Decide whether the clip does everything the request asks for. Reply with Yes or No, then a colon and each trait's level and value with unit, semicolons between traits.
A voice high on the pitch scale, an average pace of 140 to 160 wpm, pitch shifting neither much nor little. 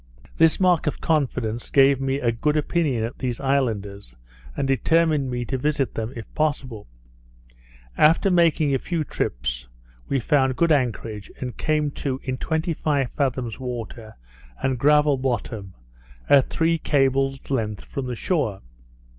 No: low, 135 Hz; average, 145 wpm; average, 4.1 semitones